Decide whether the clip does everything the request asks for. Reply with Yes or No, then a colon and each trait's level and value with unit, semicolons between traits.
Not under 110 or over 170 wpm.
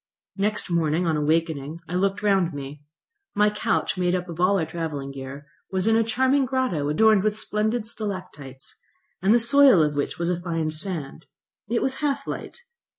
No: average, 180 wpm